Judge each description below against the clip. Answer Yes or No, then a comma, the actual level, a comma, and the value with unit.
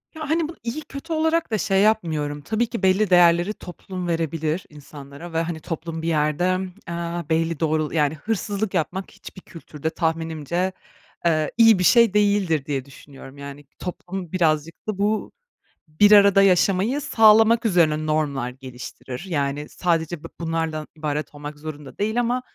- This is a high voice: No, medium, 170 Hz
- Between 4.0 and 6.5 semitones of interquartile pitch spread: Yes, average, 4.9 semitones